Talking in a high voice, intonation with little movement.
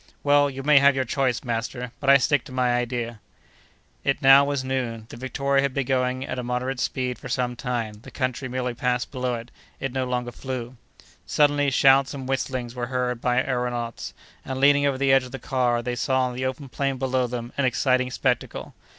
No: low, 130 Hz; narrow, 1.5 semitones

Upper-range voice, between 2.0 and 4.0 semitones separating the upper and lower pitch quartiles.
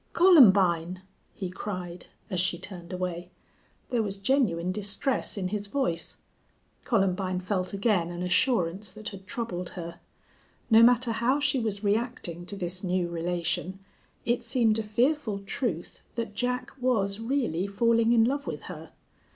No: high, 200 Hz; average, 4.4 semitones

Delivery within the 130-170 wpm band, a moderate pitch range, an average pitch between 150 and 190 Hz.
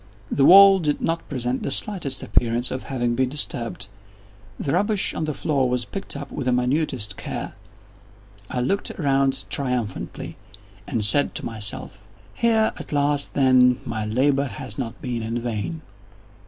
No: average, 155 wpm; average, 3.4 semitones; low, 130 Hz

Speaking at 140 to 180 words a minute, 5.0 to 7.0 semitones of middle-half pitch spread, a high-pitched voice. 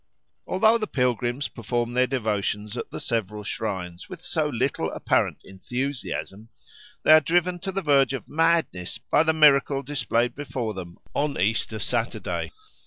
No: average, 150 wpm; wide, 5.5 semitones; low, 125 Hz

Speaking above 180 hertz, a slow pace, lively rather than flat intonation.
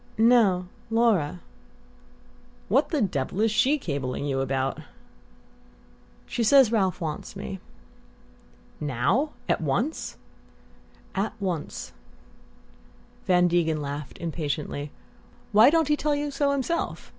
Yes: high, 190 Hz; slow, 110 wpm; wide, 8.8 semitones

